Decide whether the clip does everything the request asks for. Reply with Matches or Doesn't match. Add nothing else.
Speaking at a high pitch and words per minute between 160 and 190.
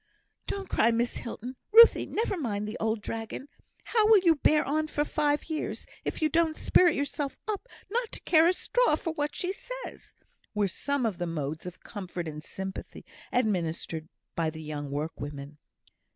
Matches